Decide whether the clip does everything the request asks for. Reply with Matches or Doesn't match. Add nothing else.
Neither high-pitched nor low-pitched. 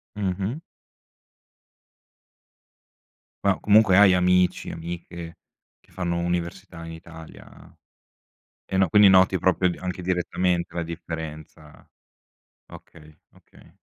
Doesn't match